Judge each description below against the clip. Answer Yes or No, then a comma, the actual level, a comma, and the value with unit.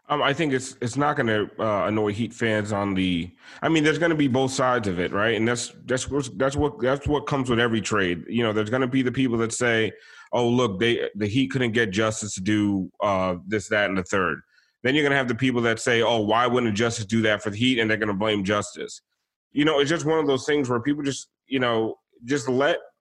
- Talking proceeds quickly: Yes, fast, 265 wpm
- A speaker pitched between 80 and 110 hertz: No, low, 120 Hz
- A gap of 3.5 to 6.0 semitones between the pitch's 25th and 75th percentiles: Yes, average, 3.8 semitones